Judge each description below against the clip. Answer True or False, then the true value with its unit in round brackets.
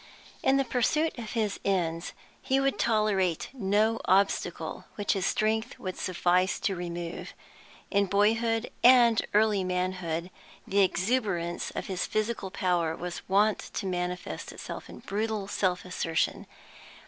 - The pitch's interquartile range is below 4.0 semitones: True (3.5 semitones)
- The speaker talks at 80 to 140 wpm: True (135 wpm)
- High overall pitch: True (195 Hz)